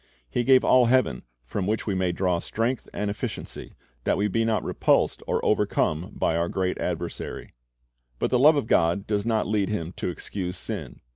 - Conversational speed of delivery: Yes, average, 190 wpm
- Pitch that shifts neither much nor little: Yes, average, 4.2 semitones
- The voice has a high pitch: No, low, 100 Hz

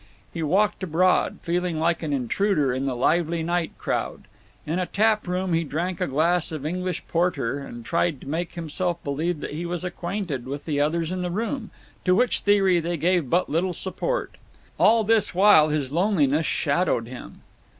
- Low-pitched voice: No, medium, 170 Hz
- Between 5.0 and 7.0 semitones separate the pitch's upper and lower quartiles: No, average, 3.4 semitones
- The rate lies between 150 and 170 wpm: No, average, 180 wpm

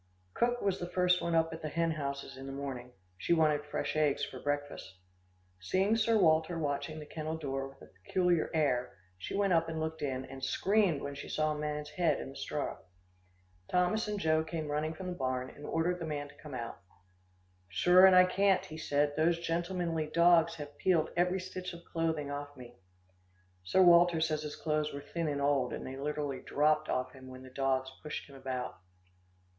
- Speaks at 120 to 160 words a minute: No, fast, 205 wpm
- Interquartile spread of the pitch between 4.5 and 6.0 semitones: No, average, 3.4 semitones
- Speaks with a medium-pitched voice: Yes, medium, 155 Hz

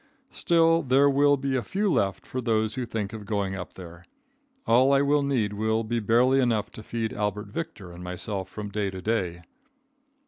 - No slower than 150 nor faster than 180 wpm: No, average, 195 wpm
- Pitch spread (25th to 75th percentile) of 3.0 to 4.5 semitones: No, average, 4.9 semitones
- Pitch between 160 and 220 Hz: No, low, 110 Hz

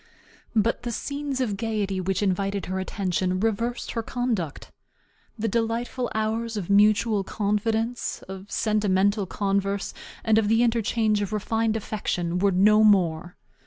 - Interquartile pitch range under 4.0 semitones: Yes, narrow, 2.6 semitones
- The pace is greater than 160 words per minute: No, slow, 135 wpm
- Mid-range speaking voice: No, high, 210 Hz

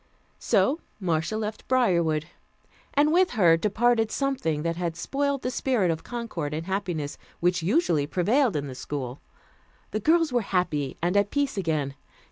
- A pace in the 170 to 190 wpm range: No, average, 155 wpm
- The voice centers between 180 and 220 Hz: Yes, high, 190 Hz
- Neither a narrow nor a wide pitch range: No, wide, 7.4 semitones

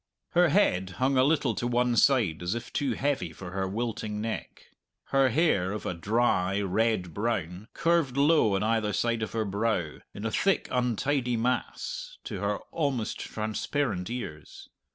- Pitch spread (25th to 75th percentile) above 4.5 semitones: Yes, average, 5.2 semitones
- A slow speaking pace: No, average, 165 wpm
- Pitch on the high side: No, low, 115 Hz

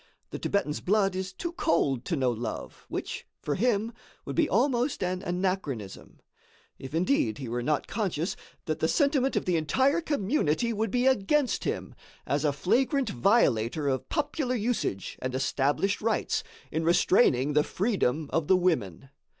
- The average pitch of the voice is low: No, medium, 185 Hz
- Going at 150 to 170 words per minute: Yes, average, 160 wpm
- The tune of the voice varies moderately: No, wide, 8.9 semitones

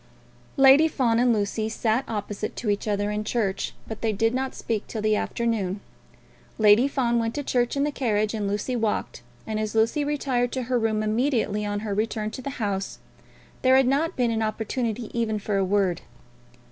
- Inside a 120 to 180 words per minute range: No, average, 195 wpm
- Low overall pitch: No, high, 225 Hz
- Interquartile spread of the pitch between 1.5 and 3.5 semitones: Yes, average, 2.9 semitones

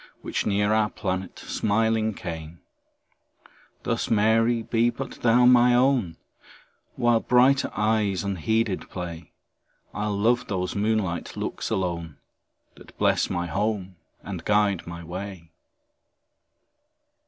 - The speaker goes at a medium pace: No, slow, 110 wpm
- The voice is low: Yes, low, 105 Hz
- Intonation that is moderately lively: Yes, average, 3.7 semitones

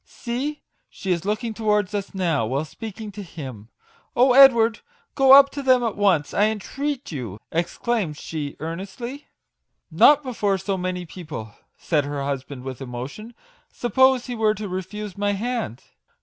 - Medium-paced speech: Yes, average, 170 wpm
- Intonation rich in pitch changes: Yes, wide, 7.1 semitones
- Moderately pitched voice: No, high, 205 Hz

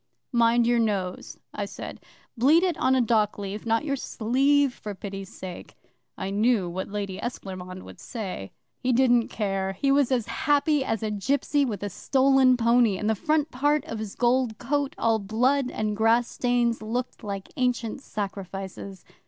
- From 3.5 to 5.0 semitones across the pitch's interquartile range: Yes, average, 4.3 semitones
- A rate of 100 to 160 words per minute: No, average, 170 wpm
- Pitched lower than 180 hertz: No, high, 230 Hz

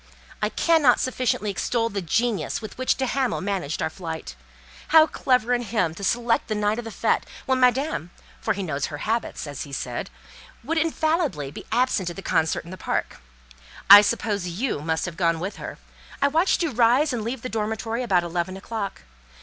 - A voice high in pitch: Yes, high, 215 Hz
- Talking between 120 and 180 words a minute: No, average, 195 wpm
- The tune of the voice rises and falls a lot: Yes, wide, 6.1 semitones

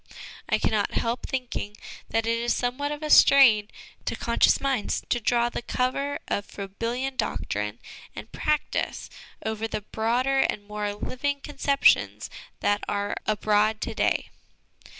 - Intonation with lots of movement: No, average, 4.2 semitones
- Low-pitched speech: No, high, 235 Hz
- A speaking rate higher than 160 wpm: No, average, 150 wpm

